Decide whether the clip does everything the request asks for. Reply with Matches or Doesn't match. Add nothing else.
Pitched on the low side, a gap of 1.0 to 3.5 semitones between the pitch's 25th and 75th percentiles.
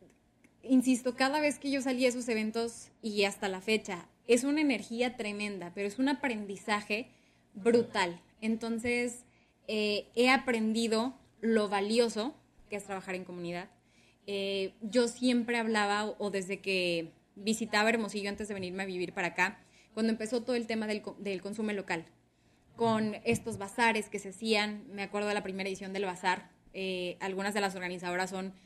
Doesn't match